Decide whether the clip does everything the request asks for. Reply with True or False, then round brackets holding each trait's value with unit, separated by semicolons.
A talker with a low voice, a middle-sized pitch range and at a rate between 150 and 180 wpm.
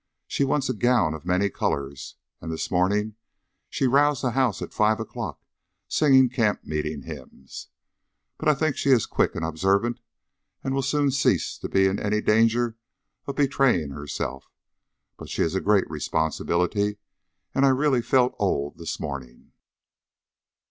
False (105 Hz; 8.2 semitones; 155 wpm)